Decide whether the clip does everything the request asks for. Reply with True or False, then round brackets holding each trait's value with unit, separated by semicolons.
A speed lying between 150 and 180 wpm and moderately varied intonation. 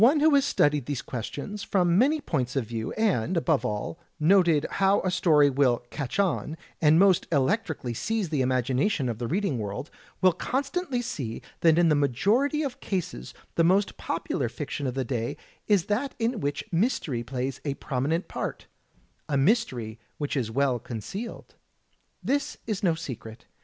False (170 wpm; 7.8 semitones)